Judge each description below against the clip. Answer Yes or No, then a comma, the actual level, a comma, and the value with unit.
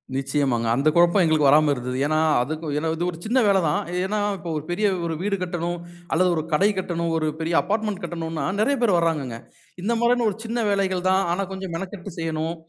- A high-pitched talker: No, medium, 175 Hz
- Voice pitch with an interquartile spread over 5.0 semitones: No, average, 3.9 semitones